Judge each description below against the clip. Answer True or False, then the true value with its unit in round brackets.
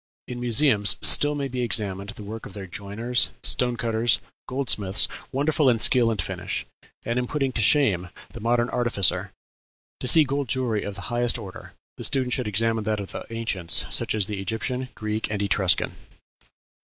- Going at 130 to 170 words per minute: False (180 wpm)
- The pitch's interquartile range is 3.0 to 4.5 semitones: True (3.5 semitones)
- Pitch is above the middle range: False (115 Hz)